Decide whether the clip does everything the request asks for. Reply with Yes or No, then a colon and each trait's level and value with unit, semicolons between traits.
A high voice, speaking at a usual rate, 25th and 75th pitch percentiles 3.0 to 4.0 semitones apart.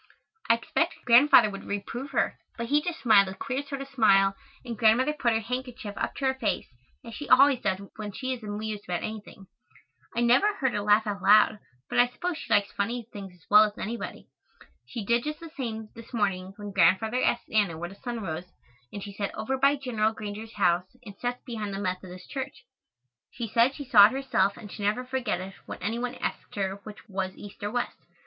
No: high, 220 Hz; fast, 215 wpm; average, 3.7 semitones